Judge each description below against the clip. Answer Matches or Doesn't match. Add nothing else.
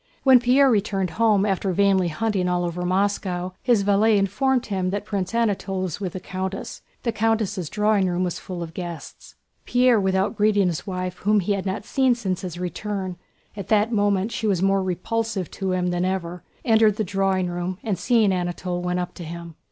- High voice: Matches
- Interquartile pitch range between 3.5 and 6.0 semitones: Doesn't match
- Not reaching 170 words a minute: Doesn't match